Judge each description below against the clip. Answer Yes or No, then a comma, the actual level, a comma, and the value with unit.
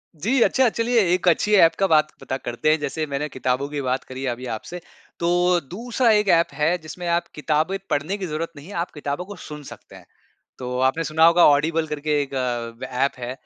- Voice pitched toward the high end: No, medium, 160 Hz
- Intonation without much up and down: No, average, 3.8 semitones